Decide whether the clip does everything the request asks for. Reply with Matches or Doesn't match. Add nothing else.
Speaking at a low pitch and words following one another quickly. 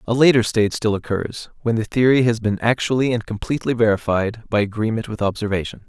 Doesn't match